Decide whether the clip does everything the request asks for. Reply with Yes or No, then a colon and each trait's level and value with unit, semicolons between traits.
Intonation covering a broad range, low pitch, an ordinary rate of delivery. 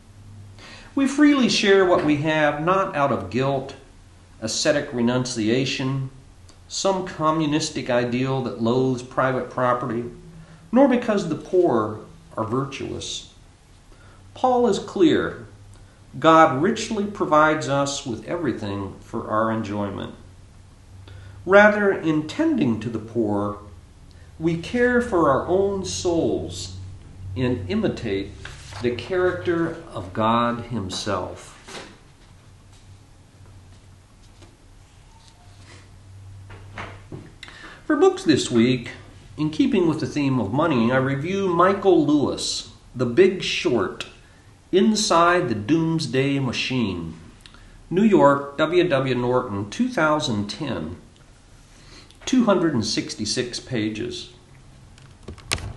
No: wide, 8.0 semitones; low, 120 Hz; slow, 95 wpm